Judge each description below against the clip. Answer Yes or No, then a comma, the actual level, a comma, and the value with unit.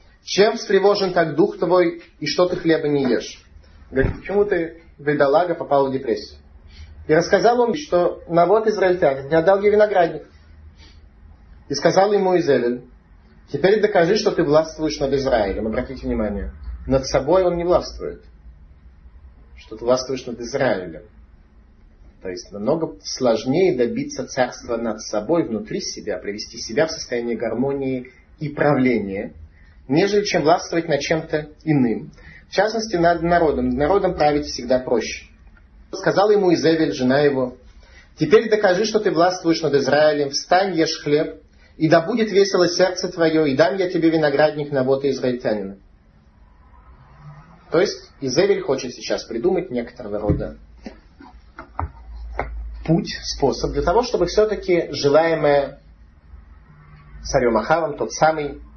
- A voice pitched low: No, medium, 145 Hz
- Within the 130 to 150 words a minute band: Yes, average, 135 wpm